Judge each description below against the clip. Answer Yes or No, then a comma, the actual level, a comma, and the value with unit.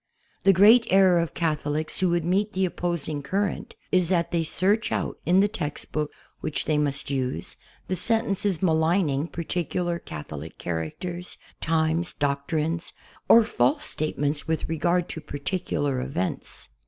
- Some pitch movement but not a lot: Yes, average, 3.9 semitones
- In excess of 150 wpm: No, average, 145 wpm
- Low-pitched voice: No, medium, 165 Hz